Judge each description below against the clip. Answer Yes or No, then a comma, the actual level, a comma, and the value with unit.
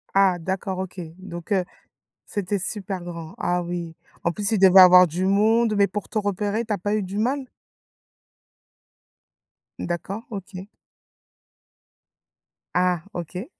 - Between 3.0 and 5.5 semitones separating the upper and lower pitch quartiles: No, narrow, 2.6 semitones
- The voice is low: No, high, 190 Hz